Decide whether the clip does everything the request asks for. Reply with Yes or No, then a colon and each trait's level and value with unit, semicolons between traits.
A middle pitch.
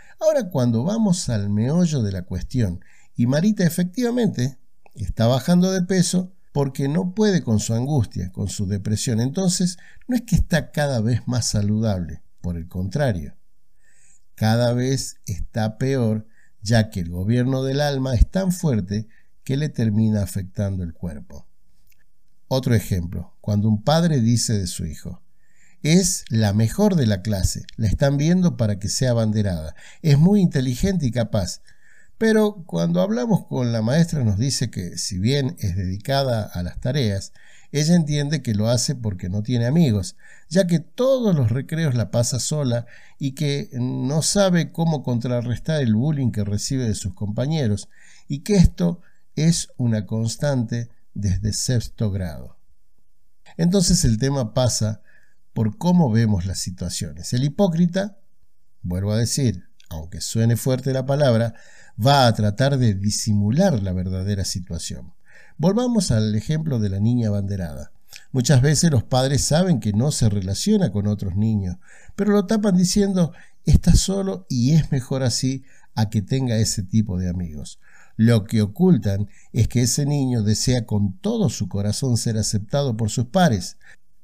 No: low, 120 Hz